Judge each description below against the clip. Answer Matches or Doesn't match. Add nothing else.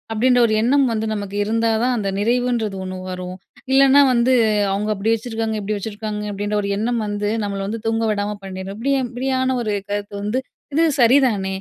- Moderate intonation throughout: Matches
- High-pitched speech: Matches